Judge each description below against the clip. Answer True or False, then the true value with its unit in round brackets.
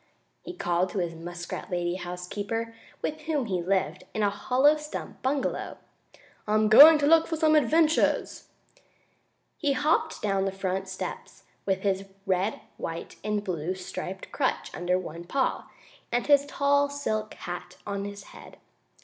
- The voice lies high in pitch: True (205 Hz)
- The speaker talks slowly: False (155 wpm)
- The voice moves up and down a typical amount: False (7.6 semitones)